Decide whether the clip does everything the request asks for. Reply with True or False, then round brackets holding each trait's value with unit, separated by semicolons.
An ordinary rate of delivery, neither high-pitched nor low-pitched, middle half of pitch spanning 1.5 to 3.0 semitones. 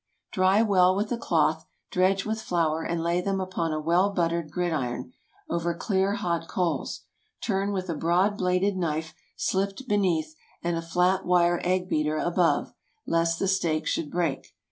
True (165 wpm; 180 Hz; 2.5 semitones)